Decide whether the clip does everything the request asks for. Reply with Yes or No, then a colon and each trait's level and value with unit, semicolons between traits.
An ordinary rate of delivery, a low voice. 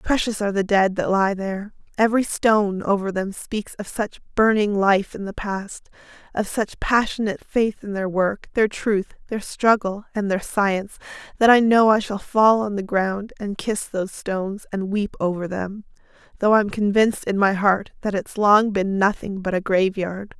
No: average, 190 wpm; high, 205 Hz